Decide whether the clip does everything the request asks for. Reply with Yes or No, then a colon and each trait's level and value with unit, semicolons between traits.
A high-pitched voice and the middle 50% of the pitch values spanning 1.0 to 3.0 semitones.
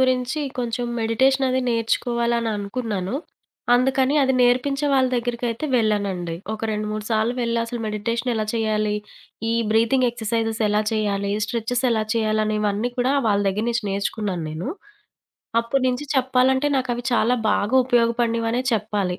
Yes: high, 230 Hz; average, 2.7 semitones